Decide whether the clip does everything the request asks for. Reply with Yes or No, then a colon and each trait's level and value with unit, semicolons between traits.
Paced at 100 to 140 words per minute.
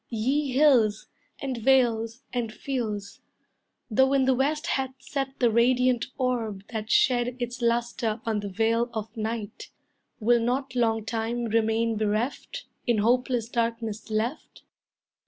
Yes: slow, 135 wpm